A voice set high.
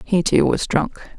No: medium, 180 Hz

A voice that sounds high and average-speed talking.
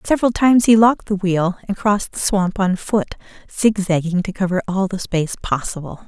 Yes: high, 195 Hz; average, 190 wpm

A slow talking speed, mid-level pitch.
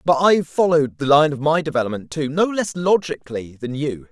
No: fast, 205 wpm; medium, 150 Hz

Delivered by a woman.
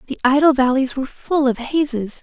Yes: female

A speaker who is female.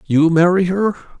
No: male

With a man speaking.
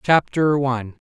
Yes: male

